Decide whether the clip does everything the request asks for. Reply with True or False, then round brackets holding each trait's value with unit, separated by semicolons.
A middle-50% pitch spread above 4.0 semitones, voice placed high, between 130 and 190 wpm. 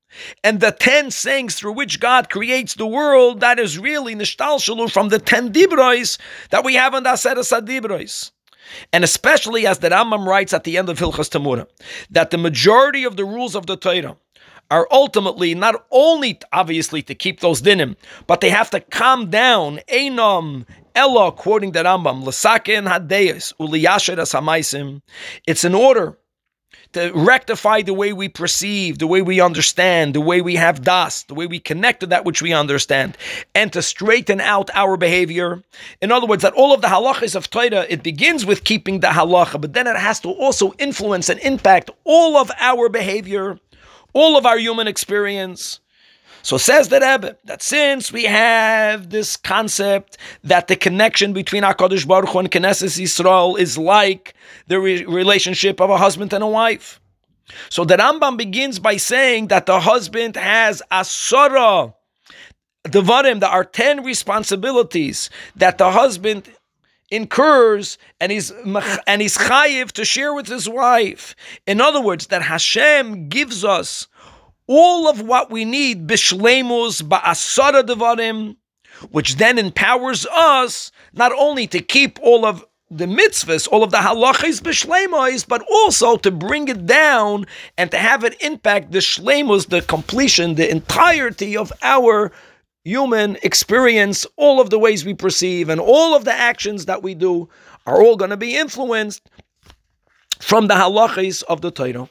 True (5.2 semitones; 210 Hz; 160 wpm)